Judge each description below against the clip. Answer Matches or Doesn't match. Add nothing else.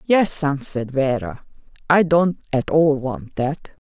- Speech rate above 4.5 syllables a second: Doesn't match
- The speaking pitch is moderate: Matches